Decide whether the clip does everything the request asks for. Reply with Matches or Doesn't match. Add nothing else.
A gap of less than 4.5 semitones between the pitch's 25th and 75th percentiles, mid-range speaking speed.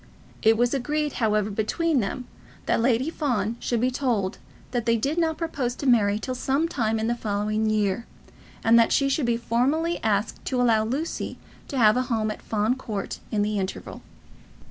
Matches